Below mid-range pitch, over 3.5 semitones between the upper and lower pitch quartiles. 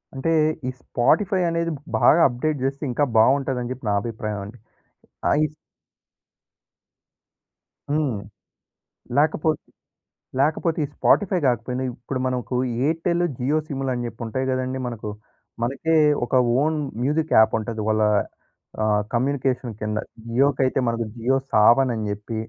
Yes: low, 130 Hz; average, 4.0 semitones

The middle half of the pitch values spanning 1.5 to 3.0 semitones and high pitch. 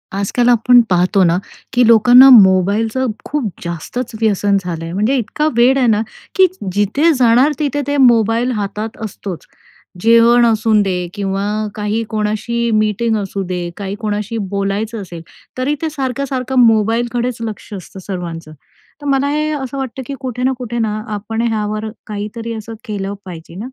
No: average, 3.7 semitones; high, 220 Hz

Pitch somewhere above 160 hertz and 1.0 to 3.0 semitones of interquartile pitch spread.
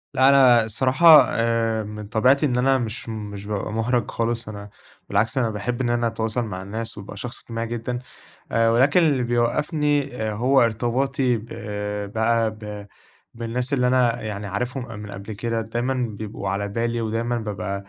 No: low, 115 Hz; narrow, 2.5 semitones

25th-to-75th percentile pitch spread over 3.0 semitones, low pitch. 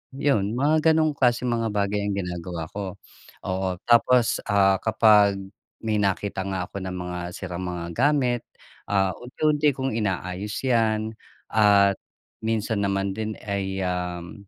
Yes: average, 3.7 semitones; low, 100 Hz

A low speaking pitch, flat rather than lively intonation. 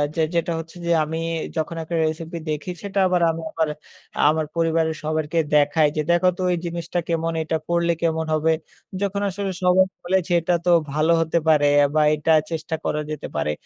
No: medium, 165 Hz; narrow, 1.7 semitones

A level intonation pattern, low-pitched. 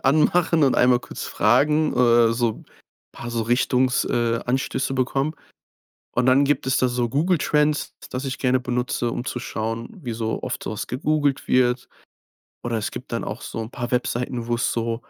Yes: narrow, 2.3 semitones; low, 125 Hz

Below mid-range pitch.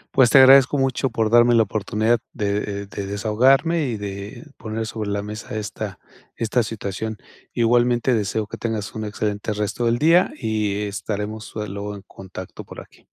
Yes: low, 110 Hz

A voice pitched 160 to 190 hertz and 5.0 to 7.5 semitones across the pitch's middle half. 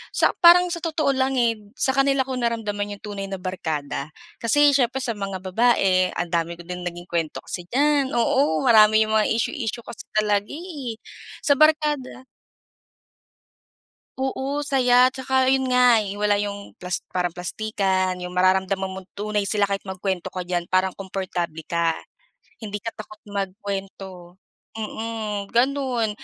No: high, 210 Hz; average, 5.3 semitones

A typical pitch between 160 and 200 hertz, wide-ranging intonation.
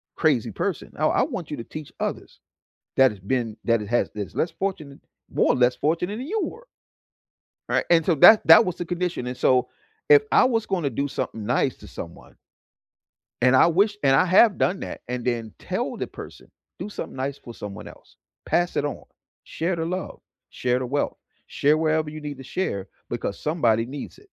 No: medium, 145 Hz; wide, 6.1 semitones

